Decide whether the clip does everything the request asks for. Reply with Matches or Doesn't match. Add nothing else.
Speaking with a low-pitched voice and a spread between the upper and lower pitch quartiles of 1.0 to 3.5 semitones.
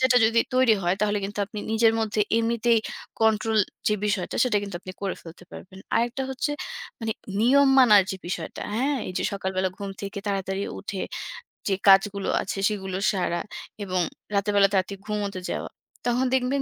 Doesn't match